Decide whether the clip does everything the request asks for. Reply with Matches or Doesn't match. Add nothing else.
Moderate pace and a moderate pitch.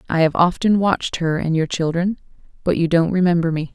Doesn't match